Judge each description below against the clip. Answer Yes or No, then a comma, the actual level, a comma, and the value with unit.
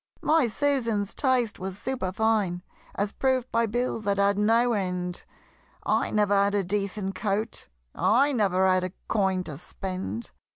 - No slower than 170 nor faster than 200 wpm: No, average, 150 wpm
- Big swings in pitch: No, average, 3.5 semitones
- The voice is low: No, high, 205 Hz